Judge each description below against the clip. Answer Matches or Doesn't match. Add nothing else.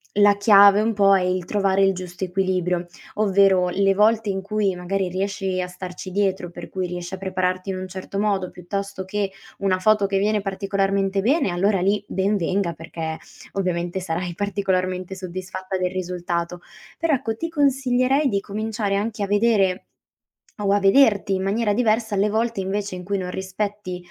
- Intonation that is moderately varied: Doesn't match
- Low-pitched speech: Doesn't match